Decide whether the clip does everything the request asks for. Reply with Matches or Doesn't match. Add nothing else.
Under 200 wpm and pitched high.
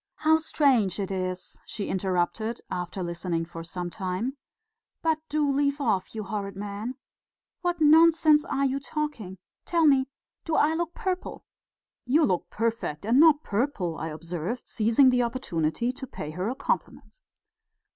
Matches